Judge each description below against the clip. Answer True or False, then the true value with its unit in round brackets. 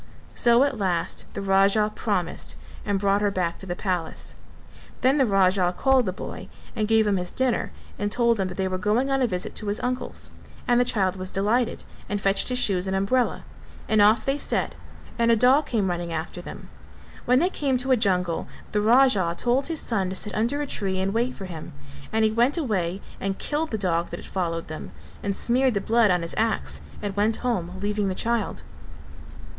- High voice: True (205 Hz)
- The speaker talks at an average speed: False (210 wpm)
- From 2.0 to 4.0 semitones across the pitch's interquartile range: False (4.4 semitones)